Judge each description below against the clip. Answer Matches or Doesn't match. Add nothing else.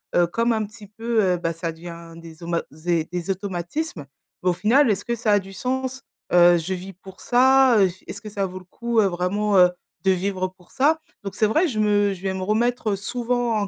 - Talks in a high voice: Matches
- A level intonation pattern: Doesn't match